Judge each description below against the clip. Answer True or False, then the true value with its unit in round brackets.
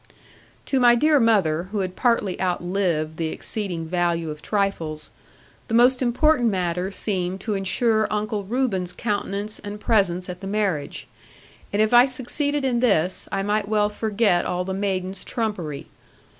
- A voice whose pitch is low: False (200 Hz)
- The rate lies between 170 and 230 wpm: False (155 wpm)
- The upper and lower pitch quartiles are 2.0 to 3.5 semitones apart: False (4.0 semitones)